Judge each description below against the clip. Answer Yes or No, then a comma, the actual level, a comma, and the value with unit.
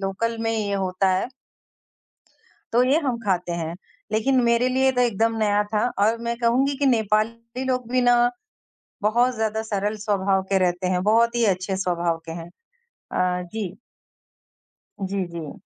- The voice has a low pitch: No, high, 215 Hz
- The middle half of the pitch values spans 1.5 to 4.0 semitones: Yes, average, 3.7 semitones